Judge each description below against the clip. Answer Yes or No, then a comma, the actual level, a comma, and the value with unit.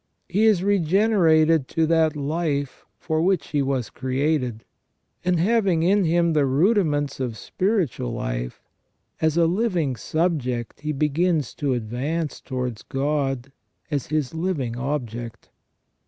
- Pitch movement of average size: Yes, average, 4.6 semitones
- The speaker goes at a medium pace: No, slow, 125 wpm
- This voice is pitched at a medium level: Yes, medium, 150 Hz